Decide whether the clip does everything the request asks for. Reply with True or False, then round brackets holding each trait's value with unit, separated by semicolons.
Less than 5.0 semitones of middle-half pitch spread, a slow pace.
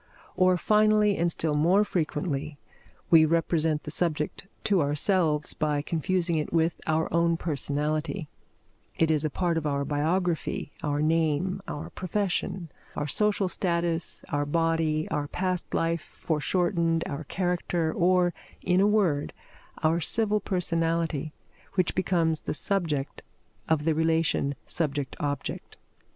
True (2.8 semitones; 130 wpm)